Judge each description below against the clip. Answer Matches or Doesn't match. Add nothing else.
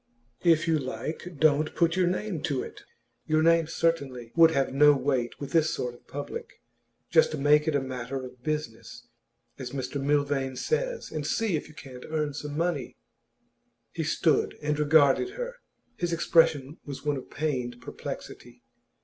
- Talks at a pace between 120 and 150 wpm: Doesn't match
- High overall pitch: Doesn't match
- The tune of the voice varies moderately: Matches